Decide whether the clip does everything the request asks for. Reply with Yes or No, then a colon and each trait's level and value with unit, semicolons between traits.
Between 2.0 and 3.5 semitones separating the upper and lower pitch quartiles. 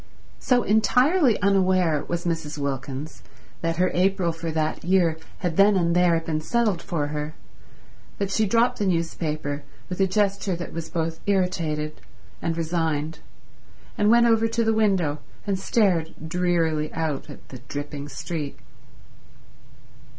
No: average, 3.9 semitones